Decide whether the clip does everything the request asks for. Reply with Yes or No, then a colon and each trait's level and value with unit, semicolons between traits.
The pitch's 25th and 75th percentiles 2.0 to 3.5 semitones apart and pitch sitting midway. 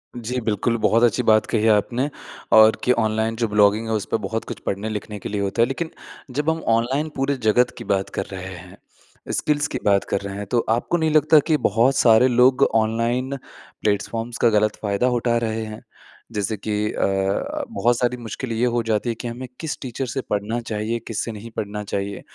No: average, 3.0 semitones; low, 115 Hz